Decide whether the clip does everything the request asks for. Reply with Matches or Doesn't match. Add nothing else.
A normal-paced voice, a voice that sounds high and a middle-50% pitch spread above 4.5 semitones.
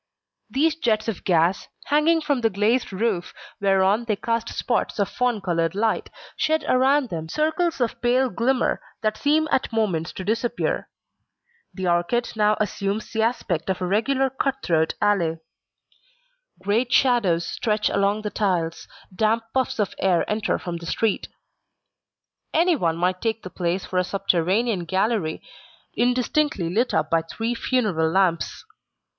Matches